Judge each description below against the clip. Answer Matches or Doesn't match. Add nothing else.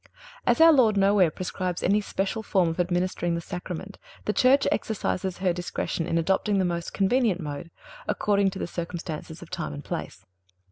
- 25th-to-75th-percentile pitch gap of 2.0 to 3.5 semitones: Matches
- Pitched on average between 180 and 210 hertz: Matches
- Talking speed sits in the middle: Matches